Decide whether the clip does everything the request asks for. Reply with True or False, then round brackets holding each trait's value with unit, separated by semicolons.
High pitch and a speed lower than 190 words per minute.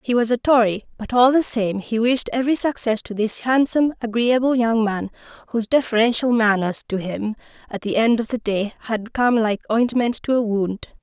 False (230 Hz; 195 wpm)